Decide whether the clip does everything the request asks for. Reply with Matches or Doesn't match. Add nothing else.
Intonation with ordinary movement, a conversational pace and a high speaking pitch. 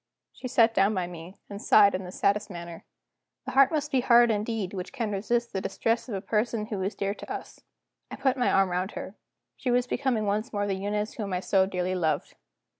Doesn't match